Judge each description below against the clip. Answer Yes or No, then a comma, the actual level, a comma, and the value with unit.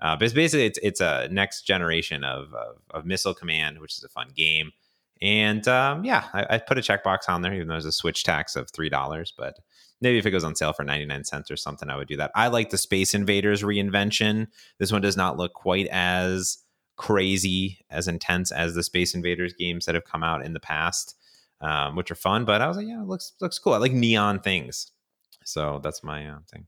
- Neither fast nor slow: No, fast, 235 wpm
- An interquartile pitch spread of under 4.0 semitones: No, average, 4.5 semitones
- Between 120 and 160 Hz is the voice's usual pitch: No, very low, 90 Hz